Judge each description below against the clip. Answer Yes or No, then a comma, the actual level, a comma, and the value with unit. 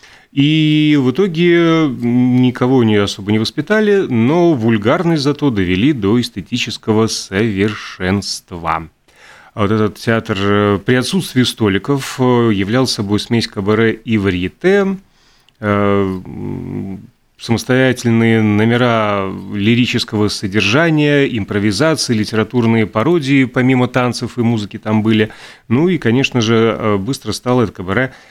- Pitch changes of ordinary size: Yes, average, 3.7 semitones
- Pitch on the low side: Yes, low, 115 Hz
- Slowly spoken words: Yes, slow, 100 wpm